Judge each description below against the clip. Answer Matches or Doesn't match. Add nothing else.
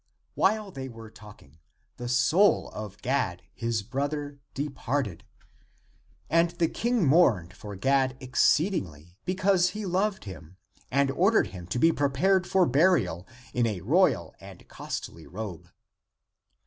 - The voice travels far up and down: Matches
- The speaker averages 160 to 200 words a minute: Doesn't match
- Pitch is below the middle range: Matches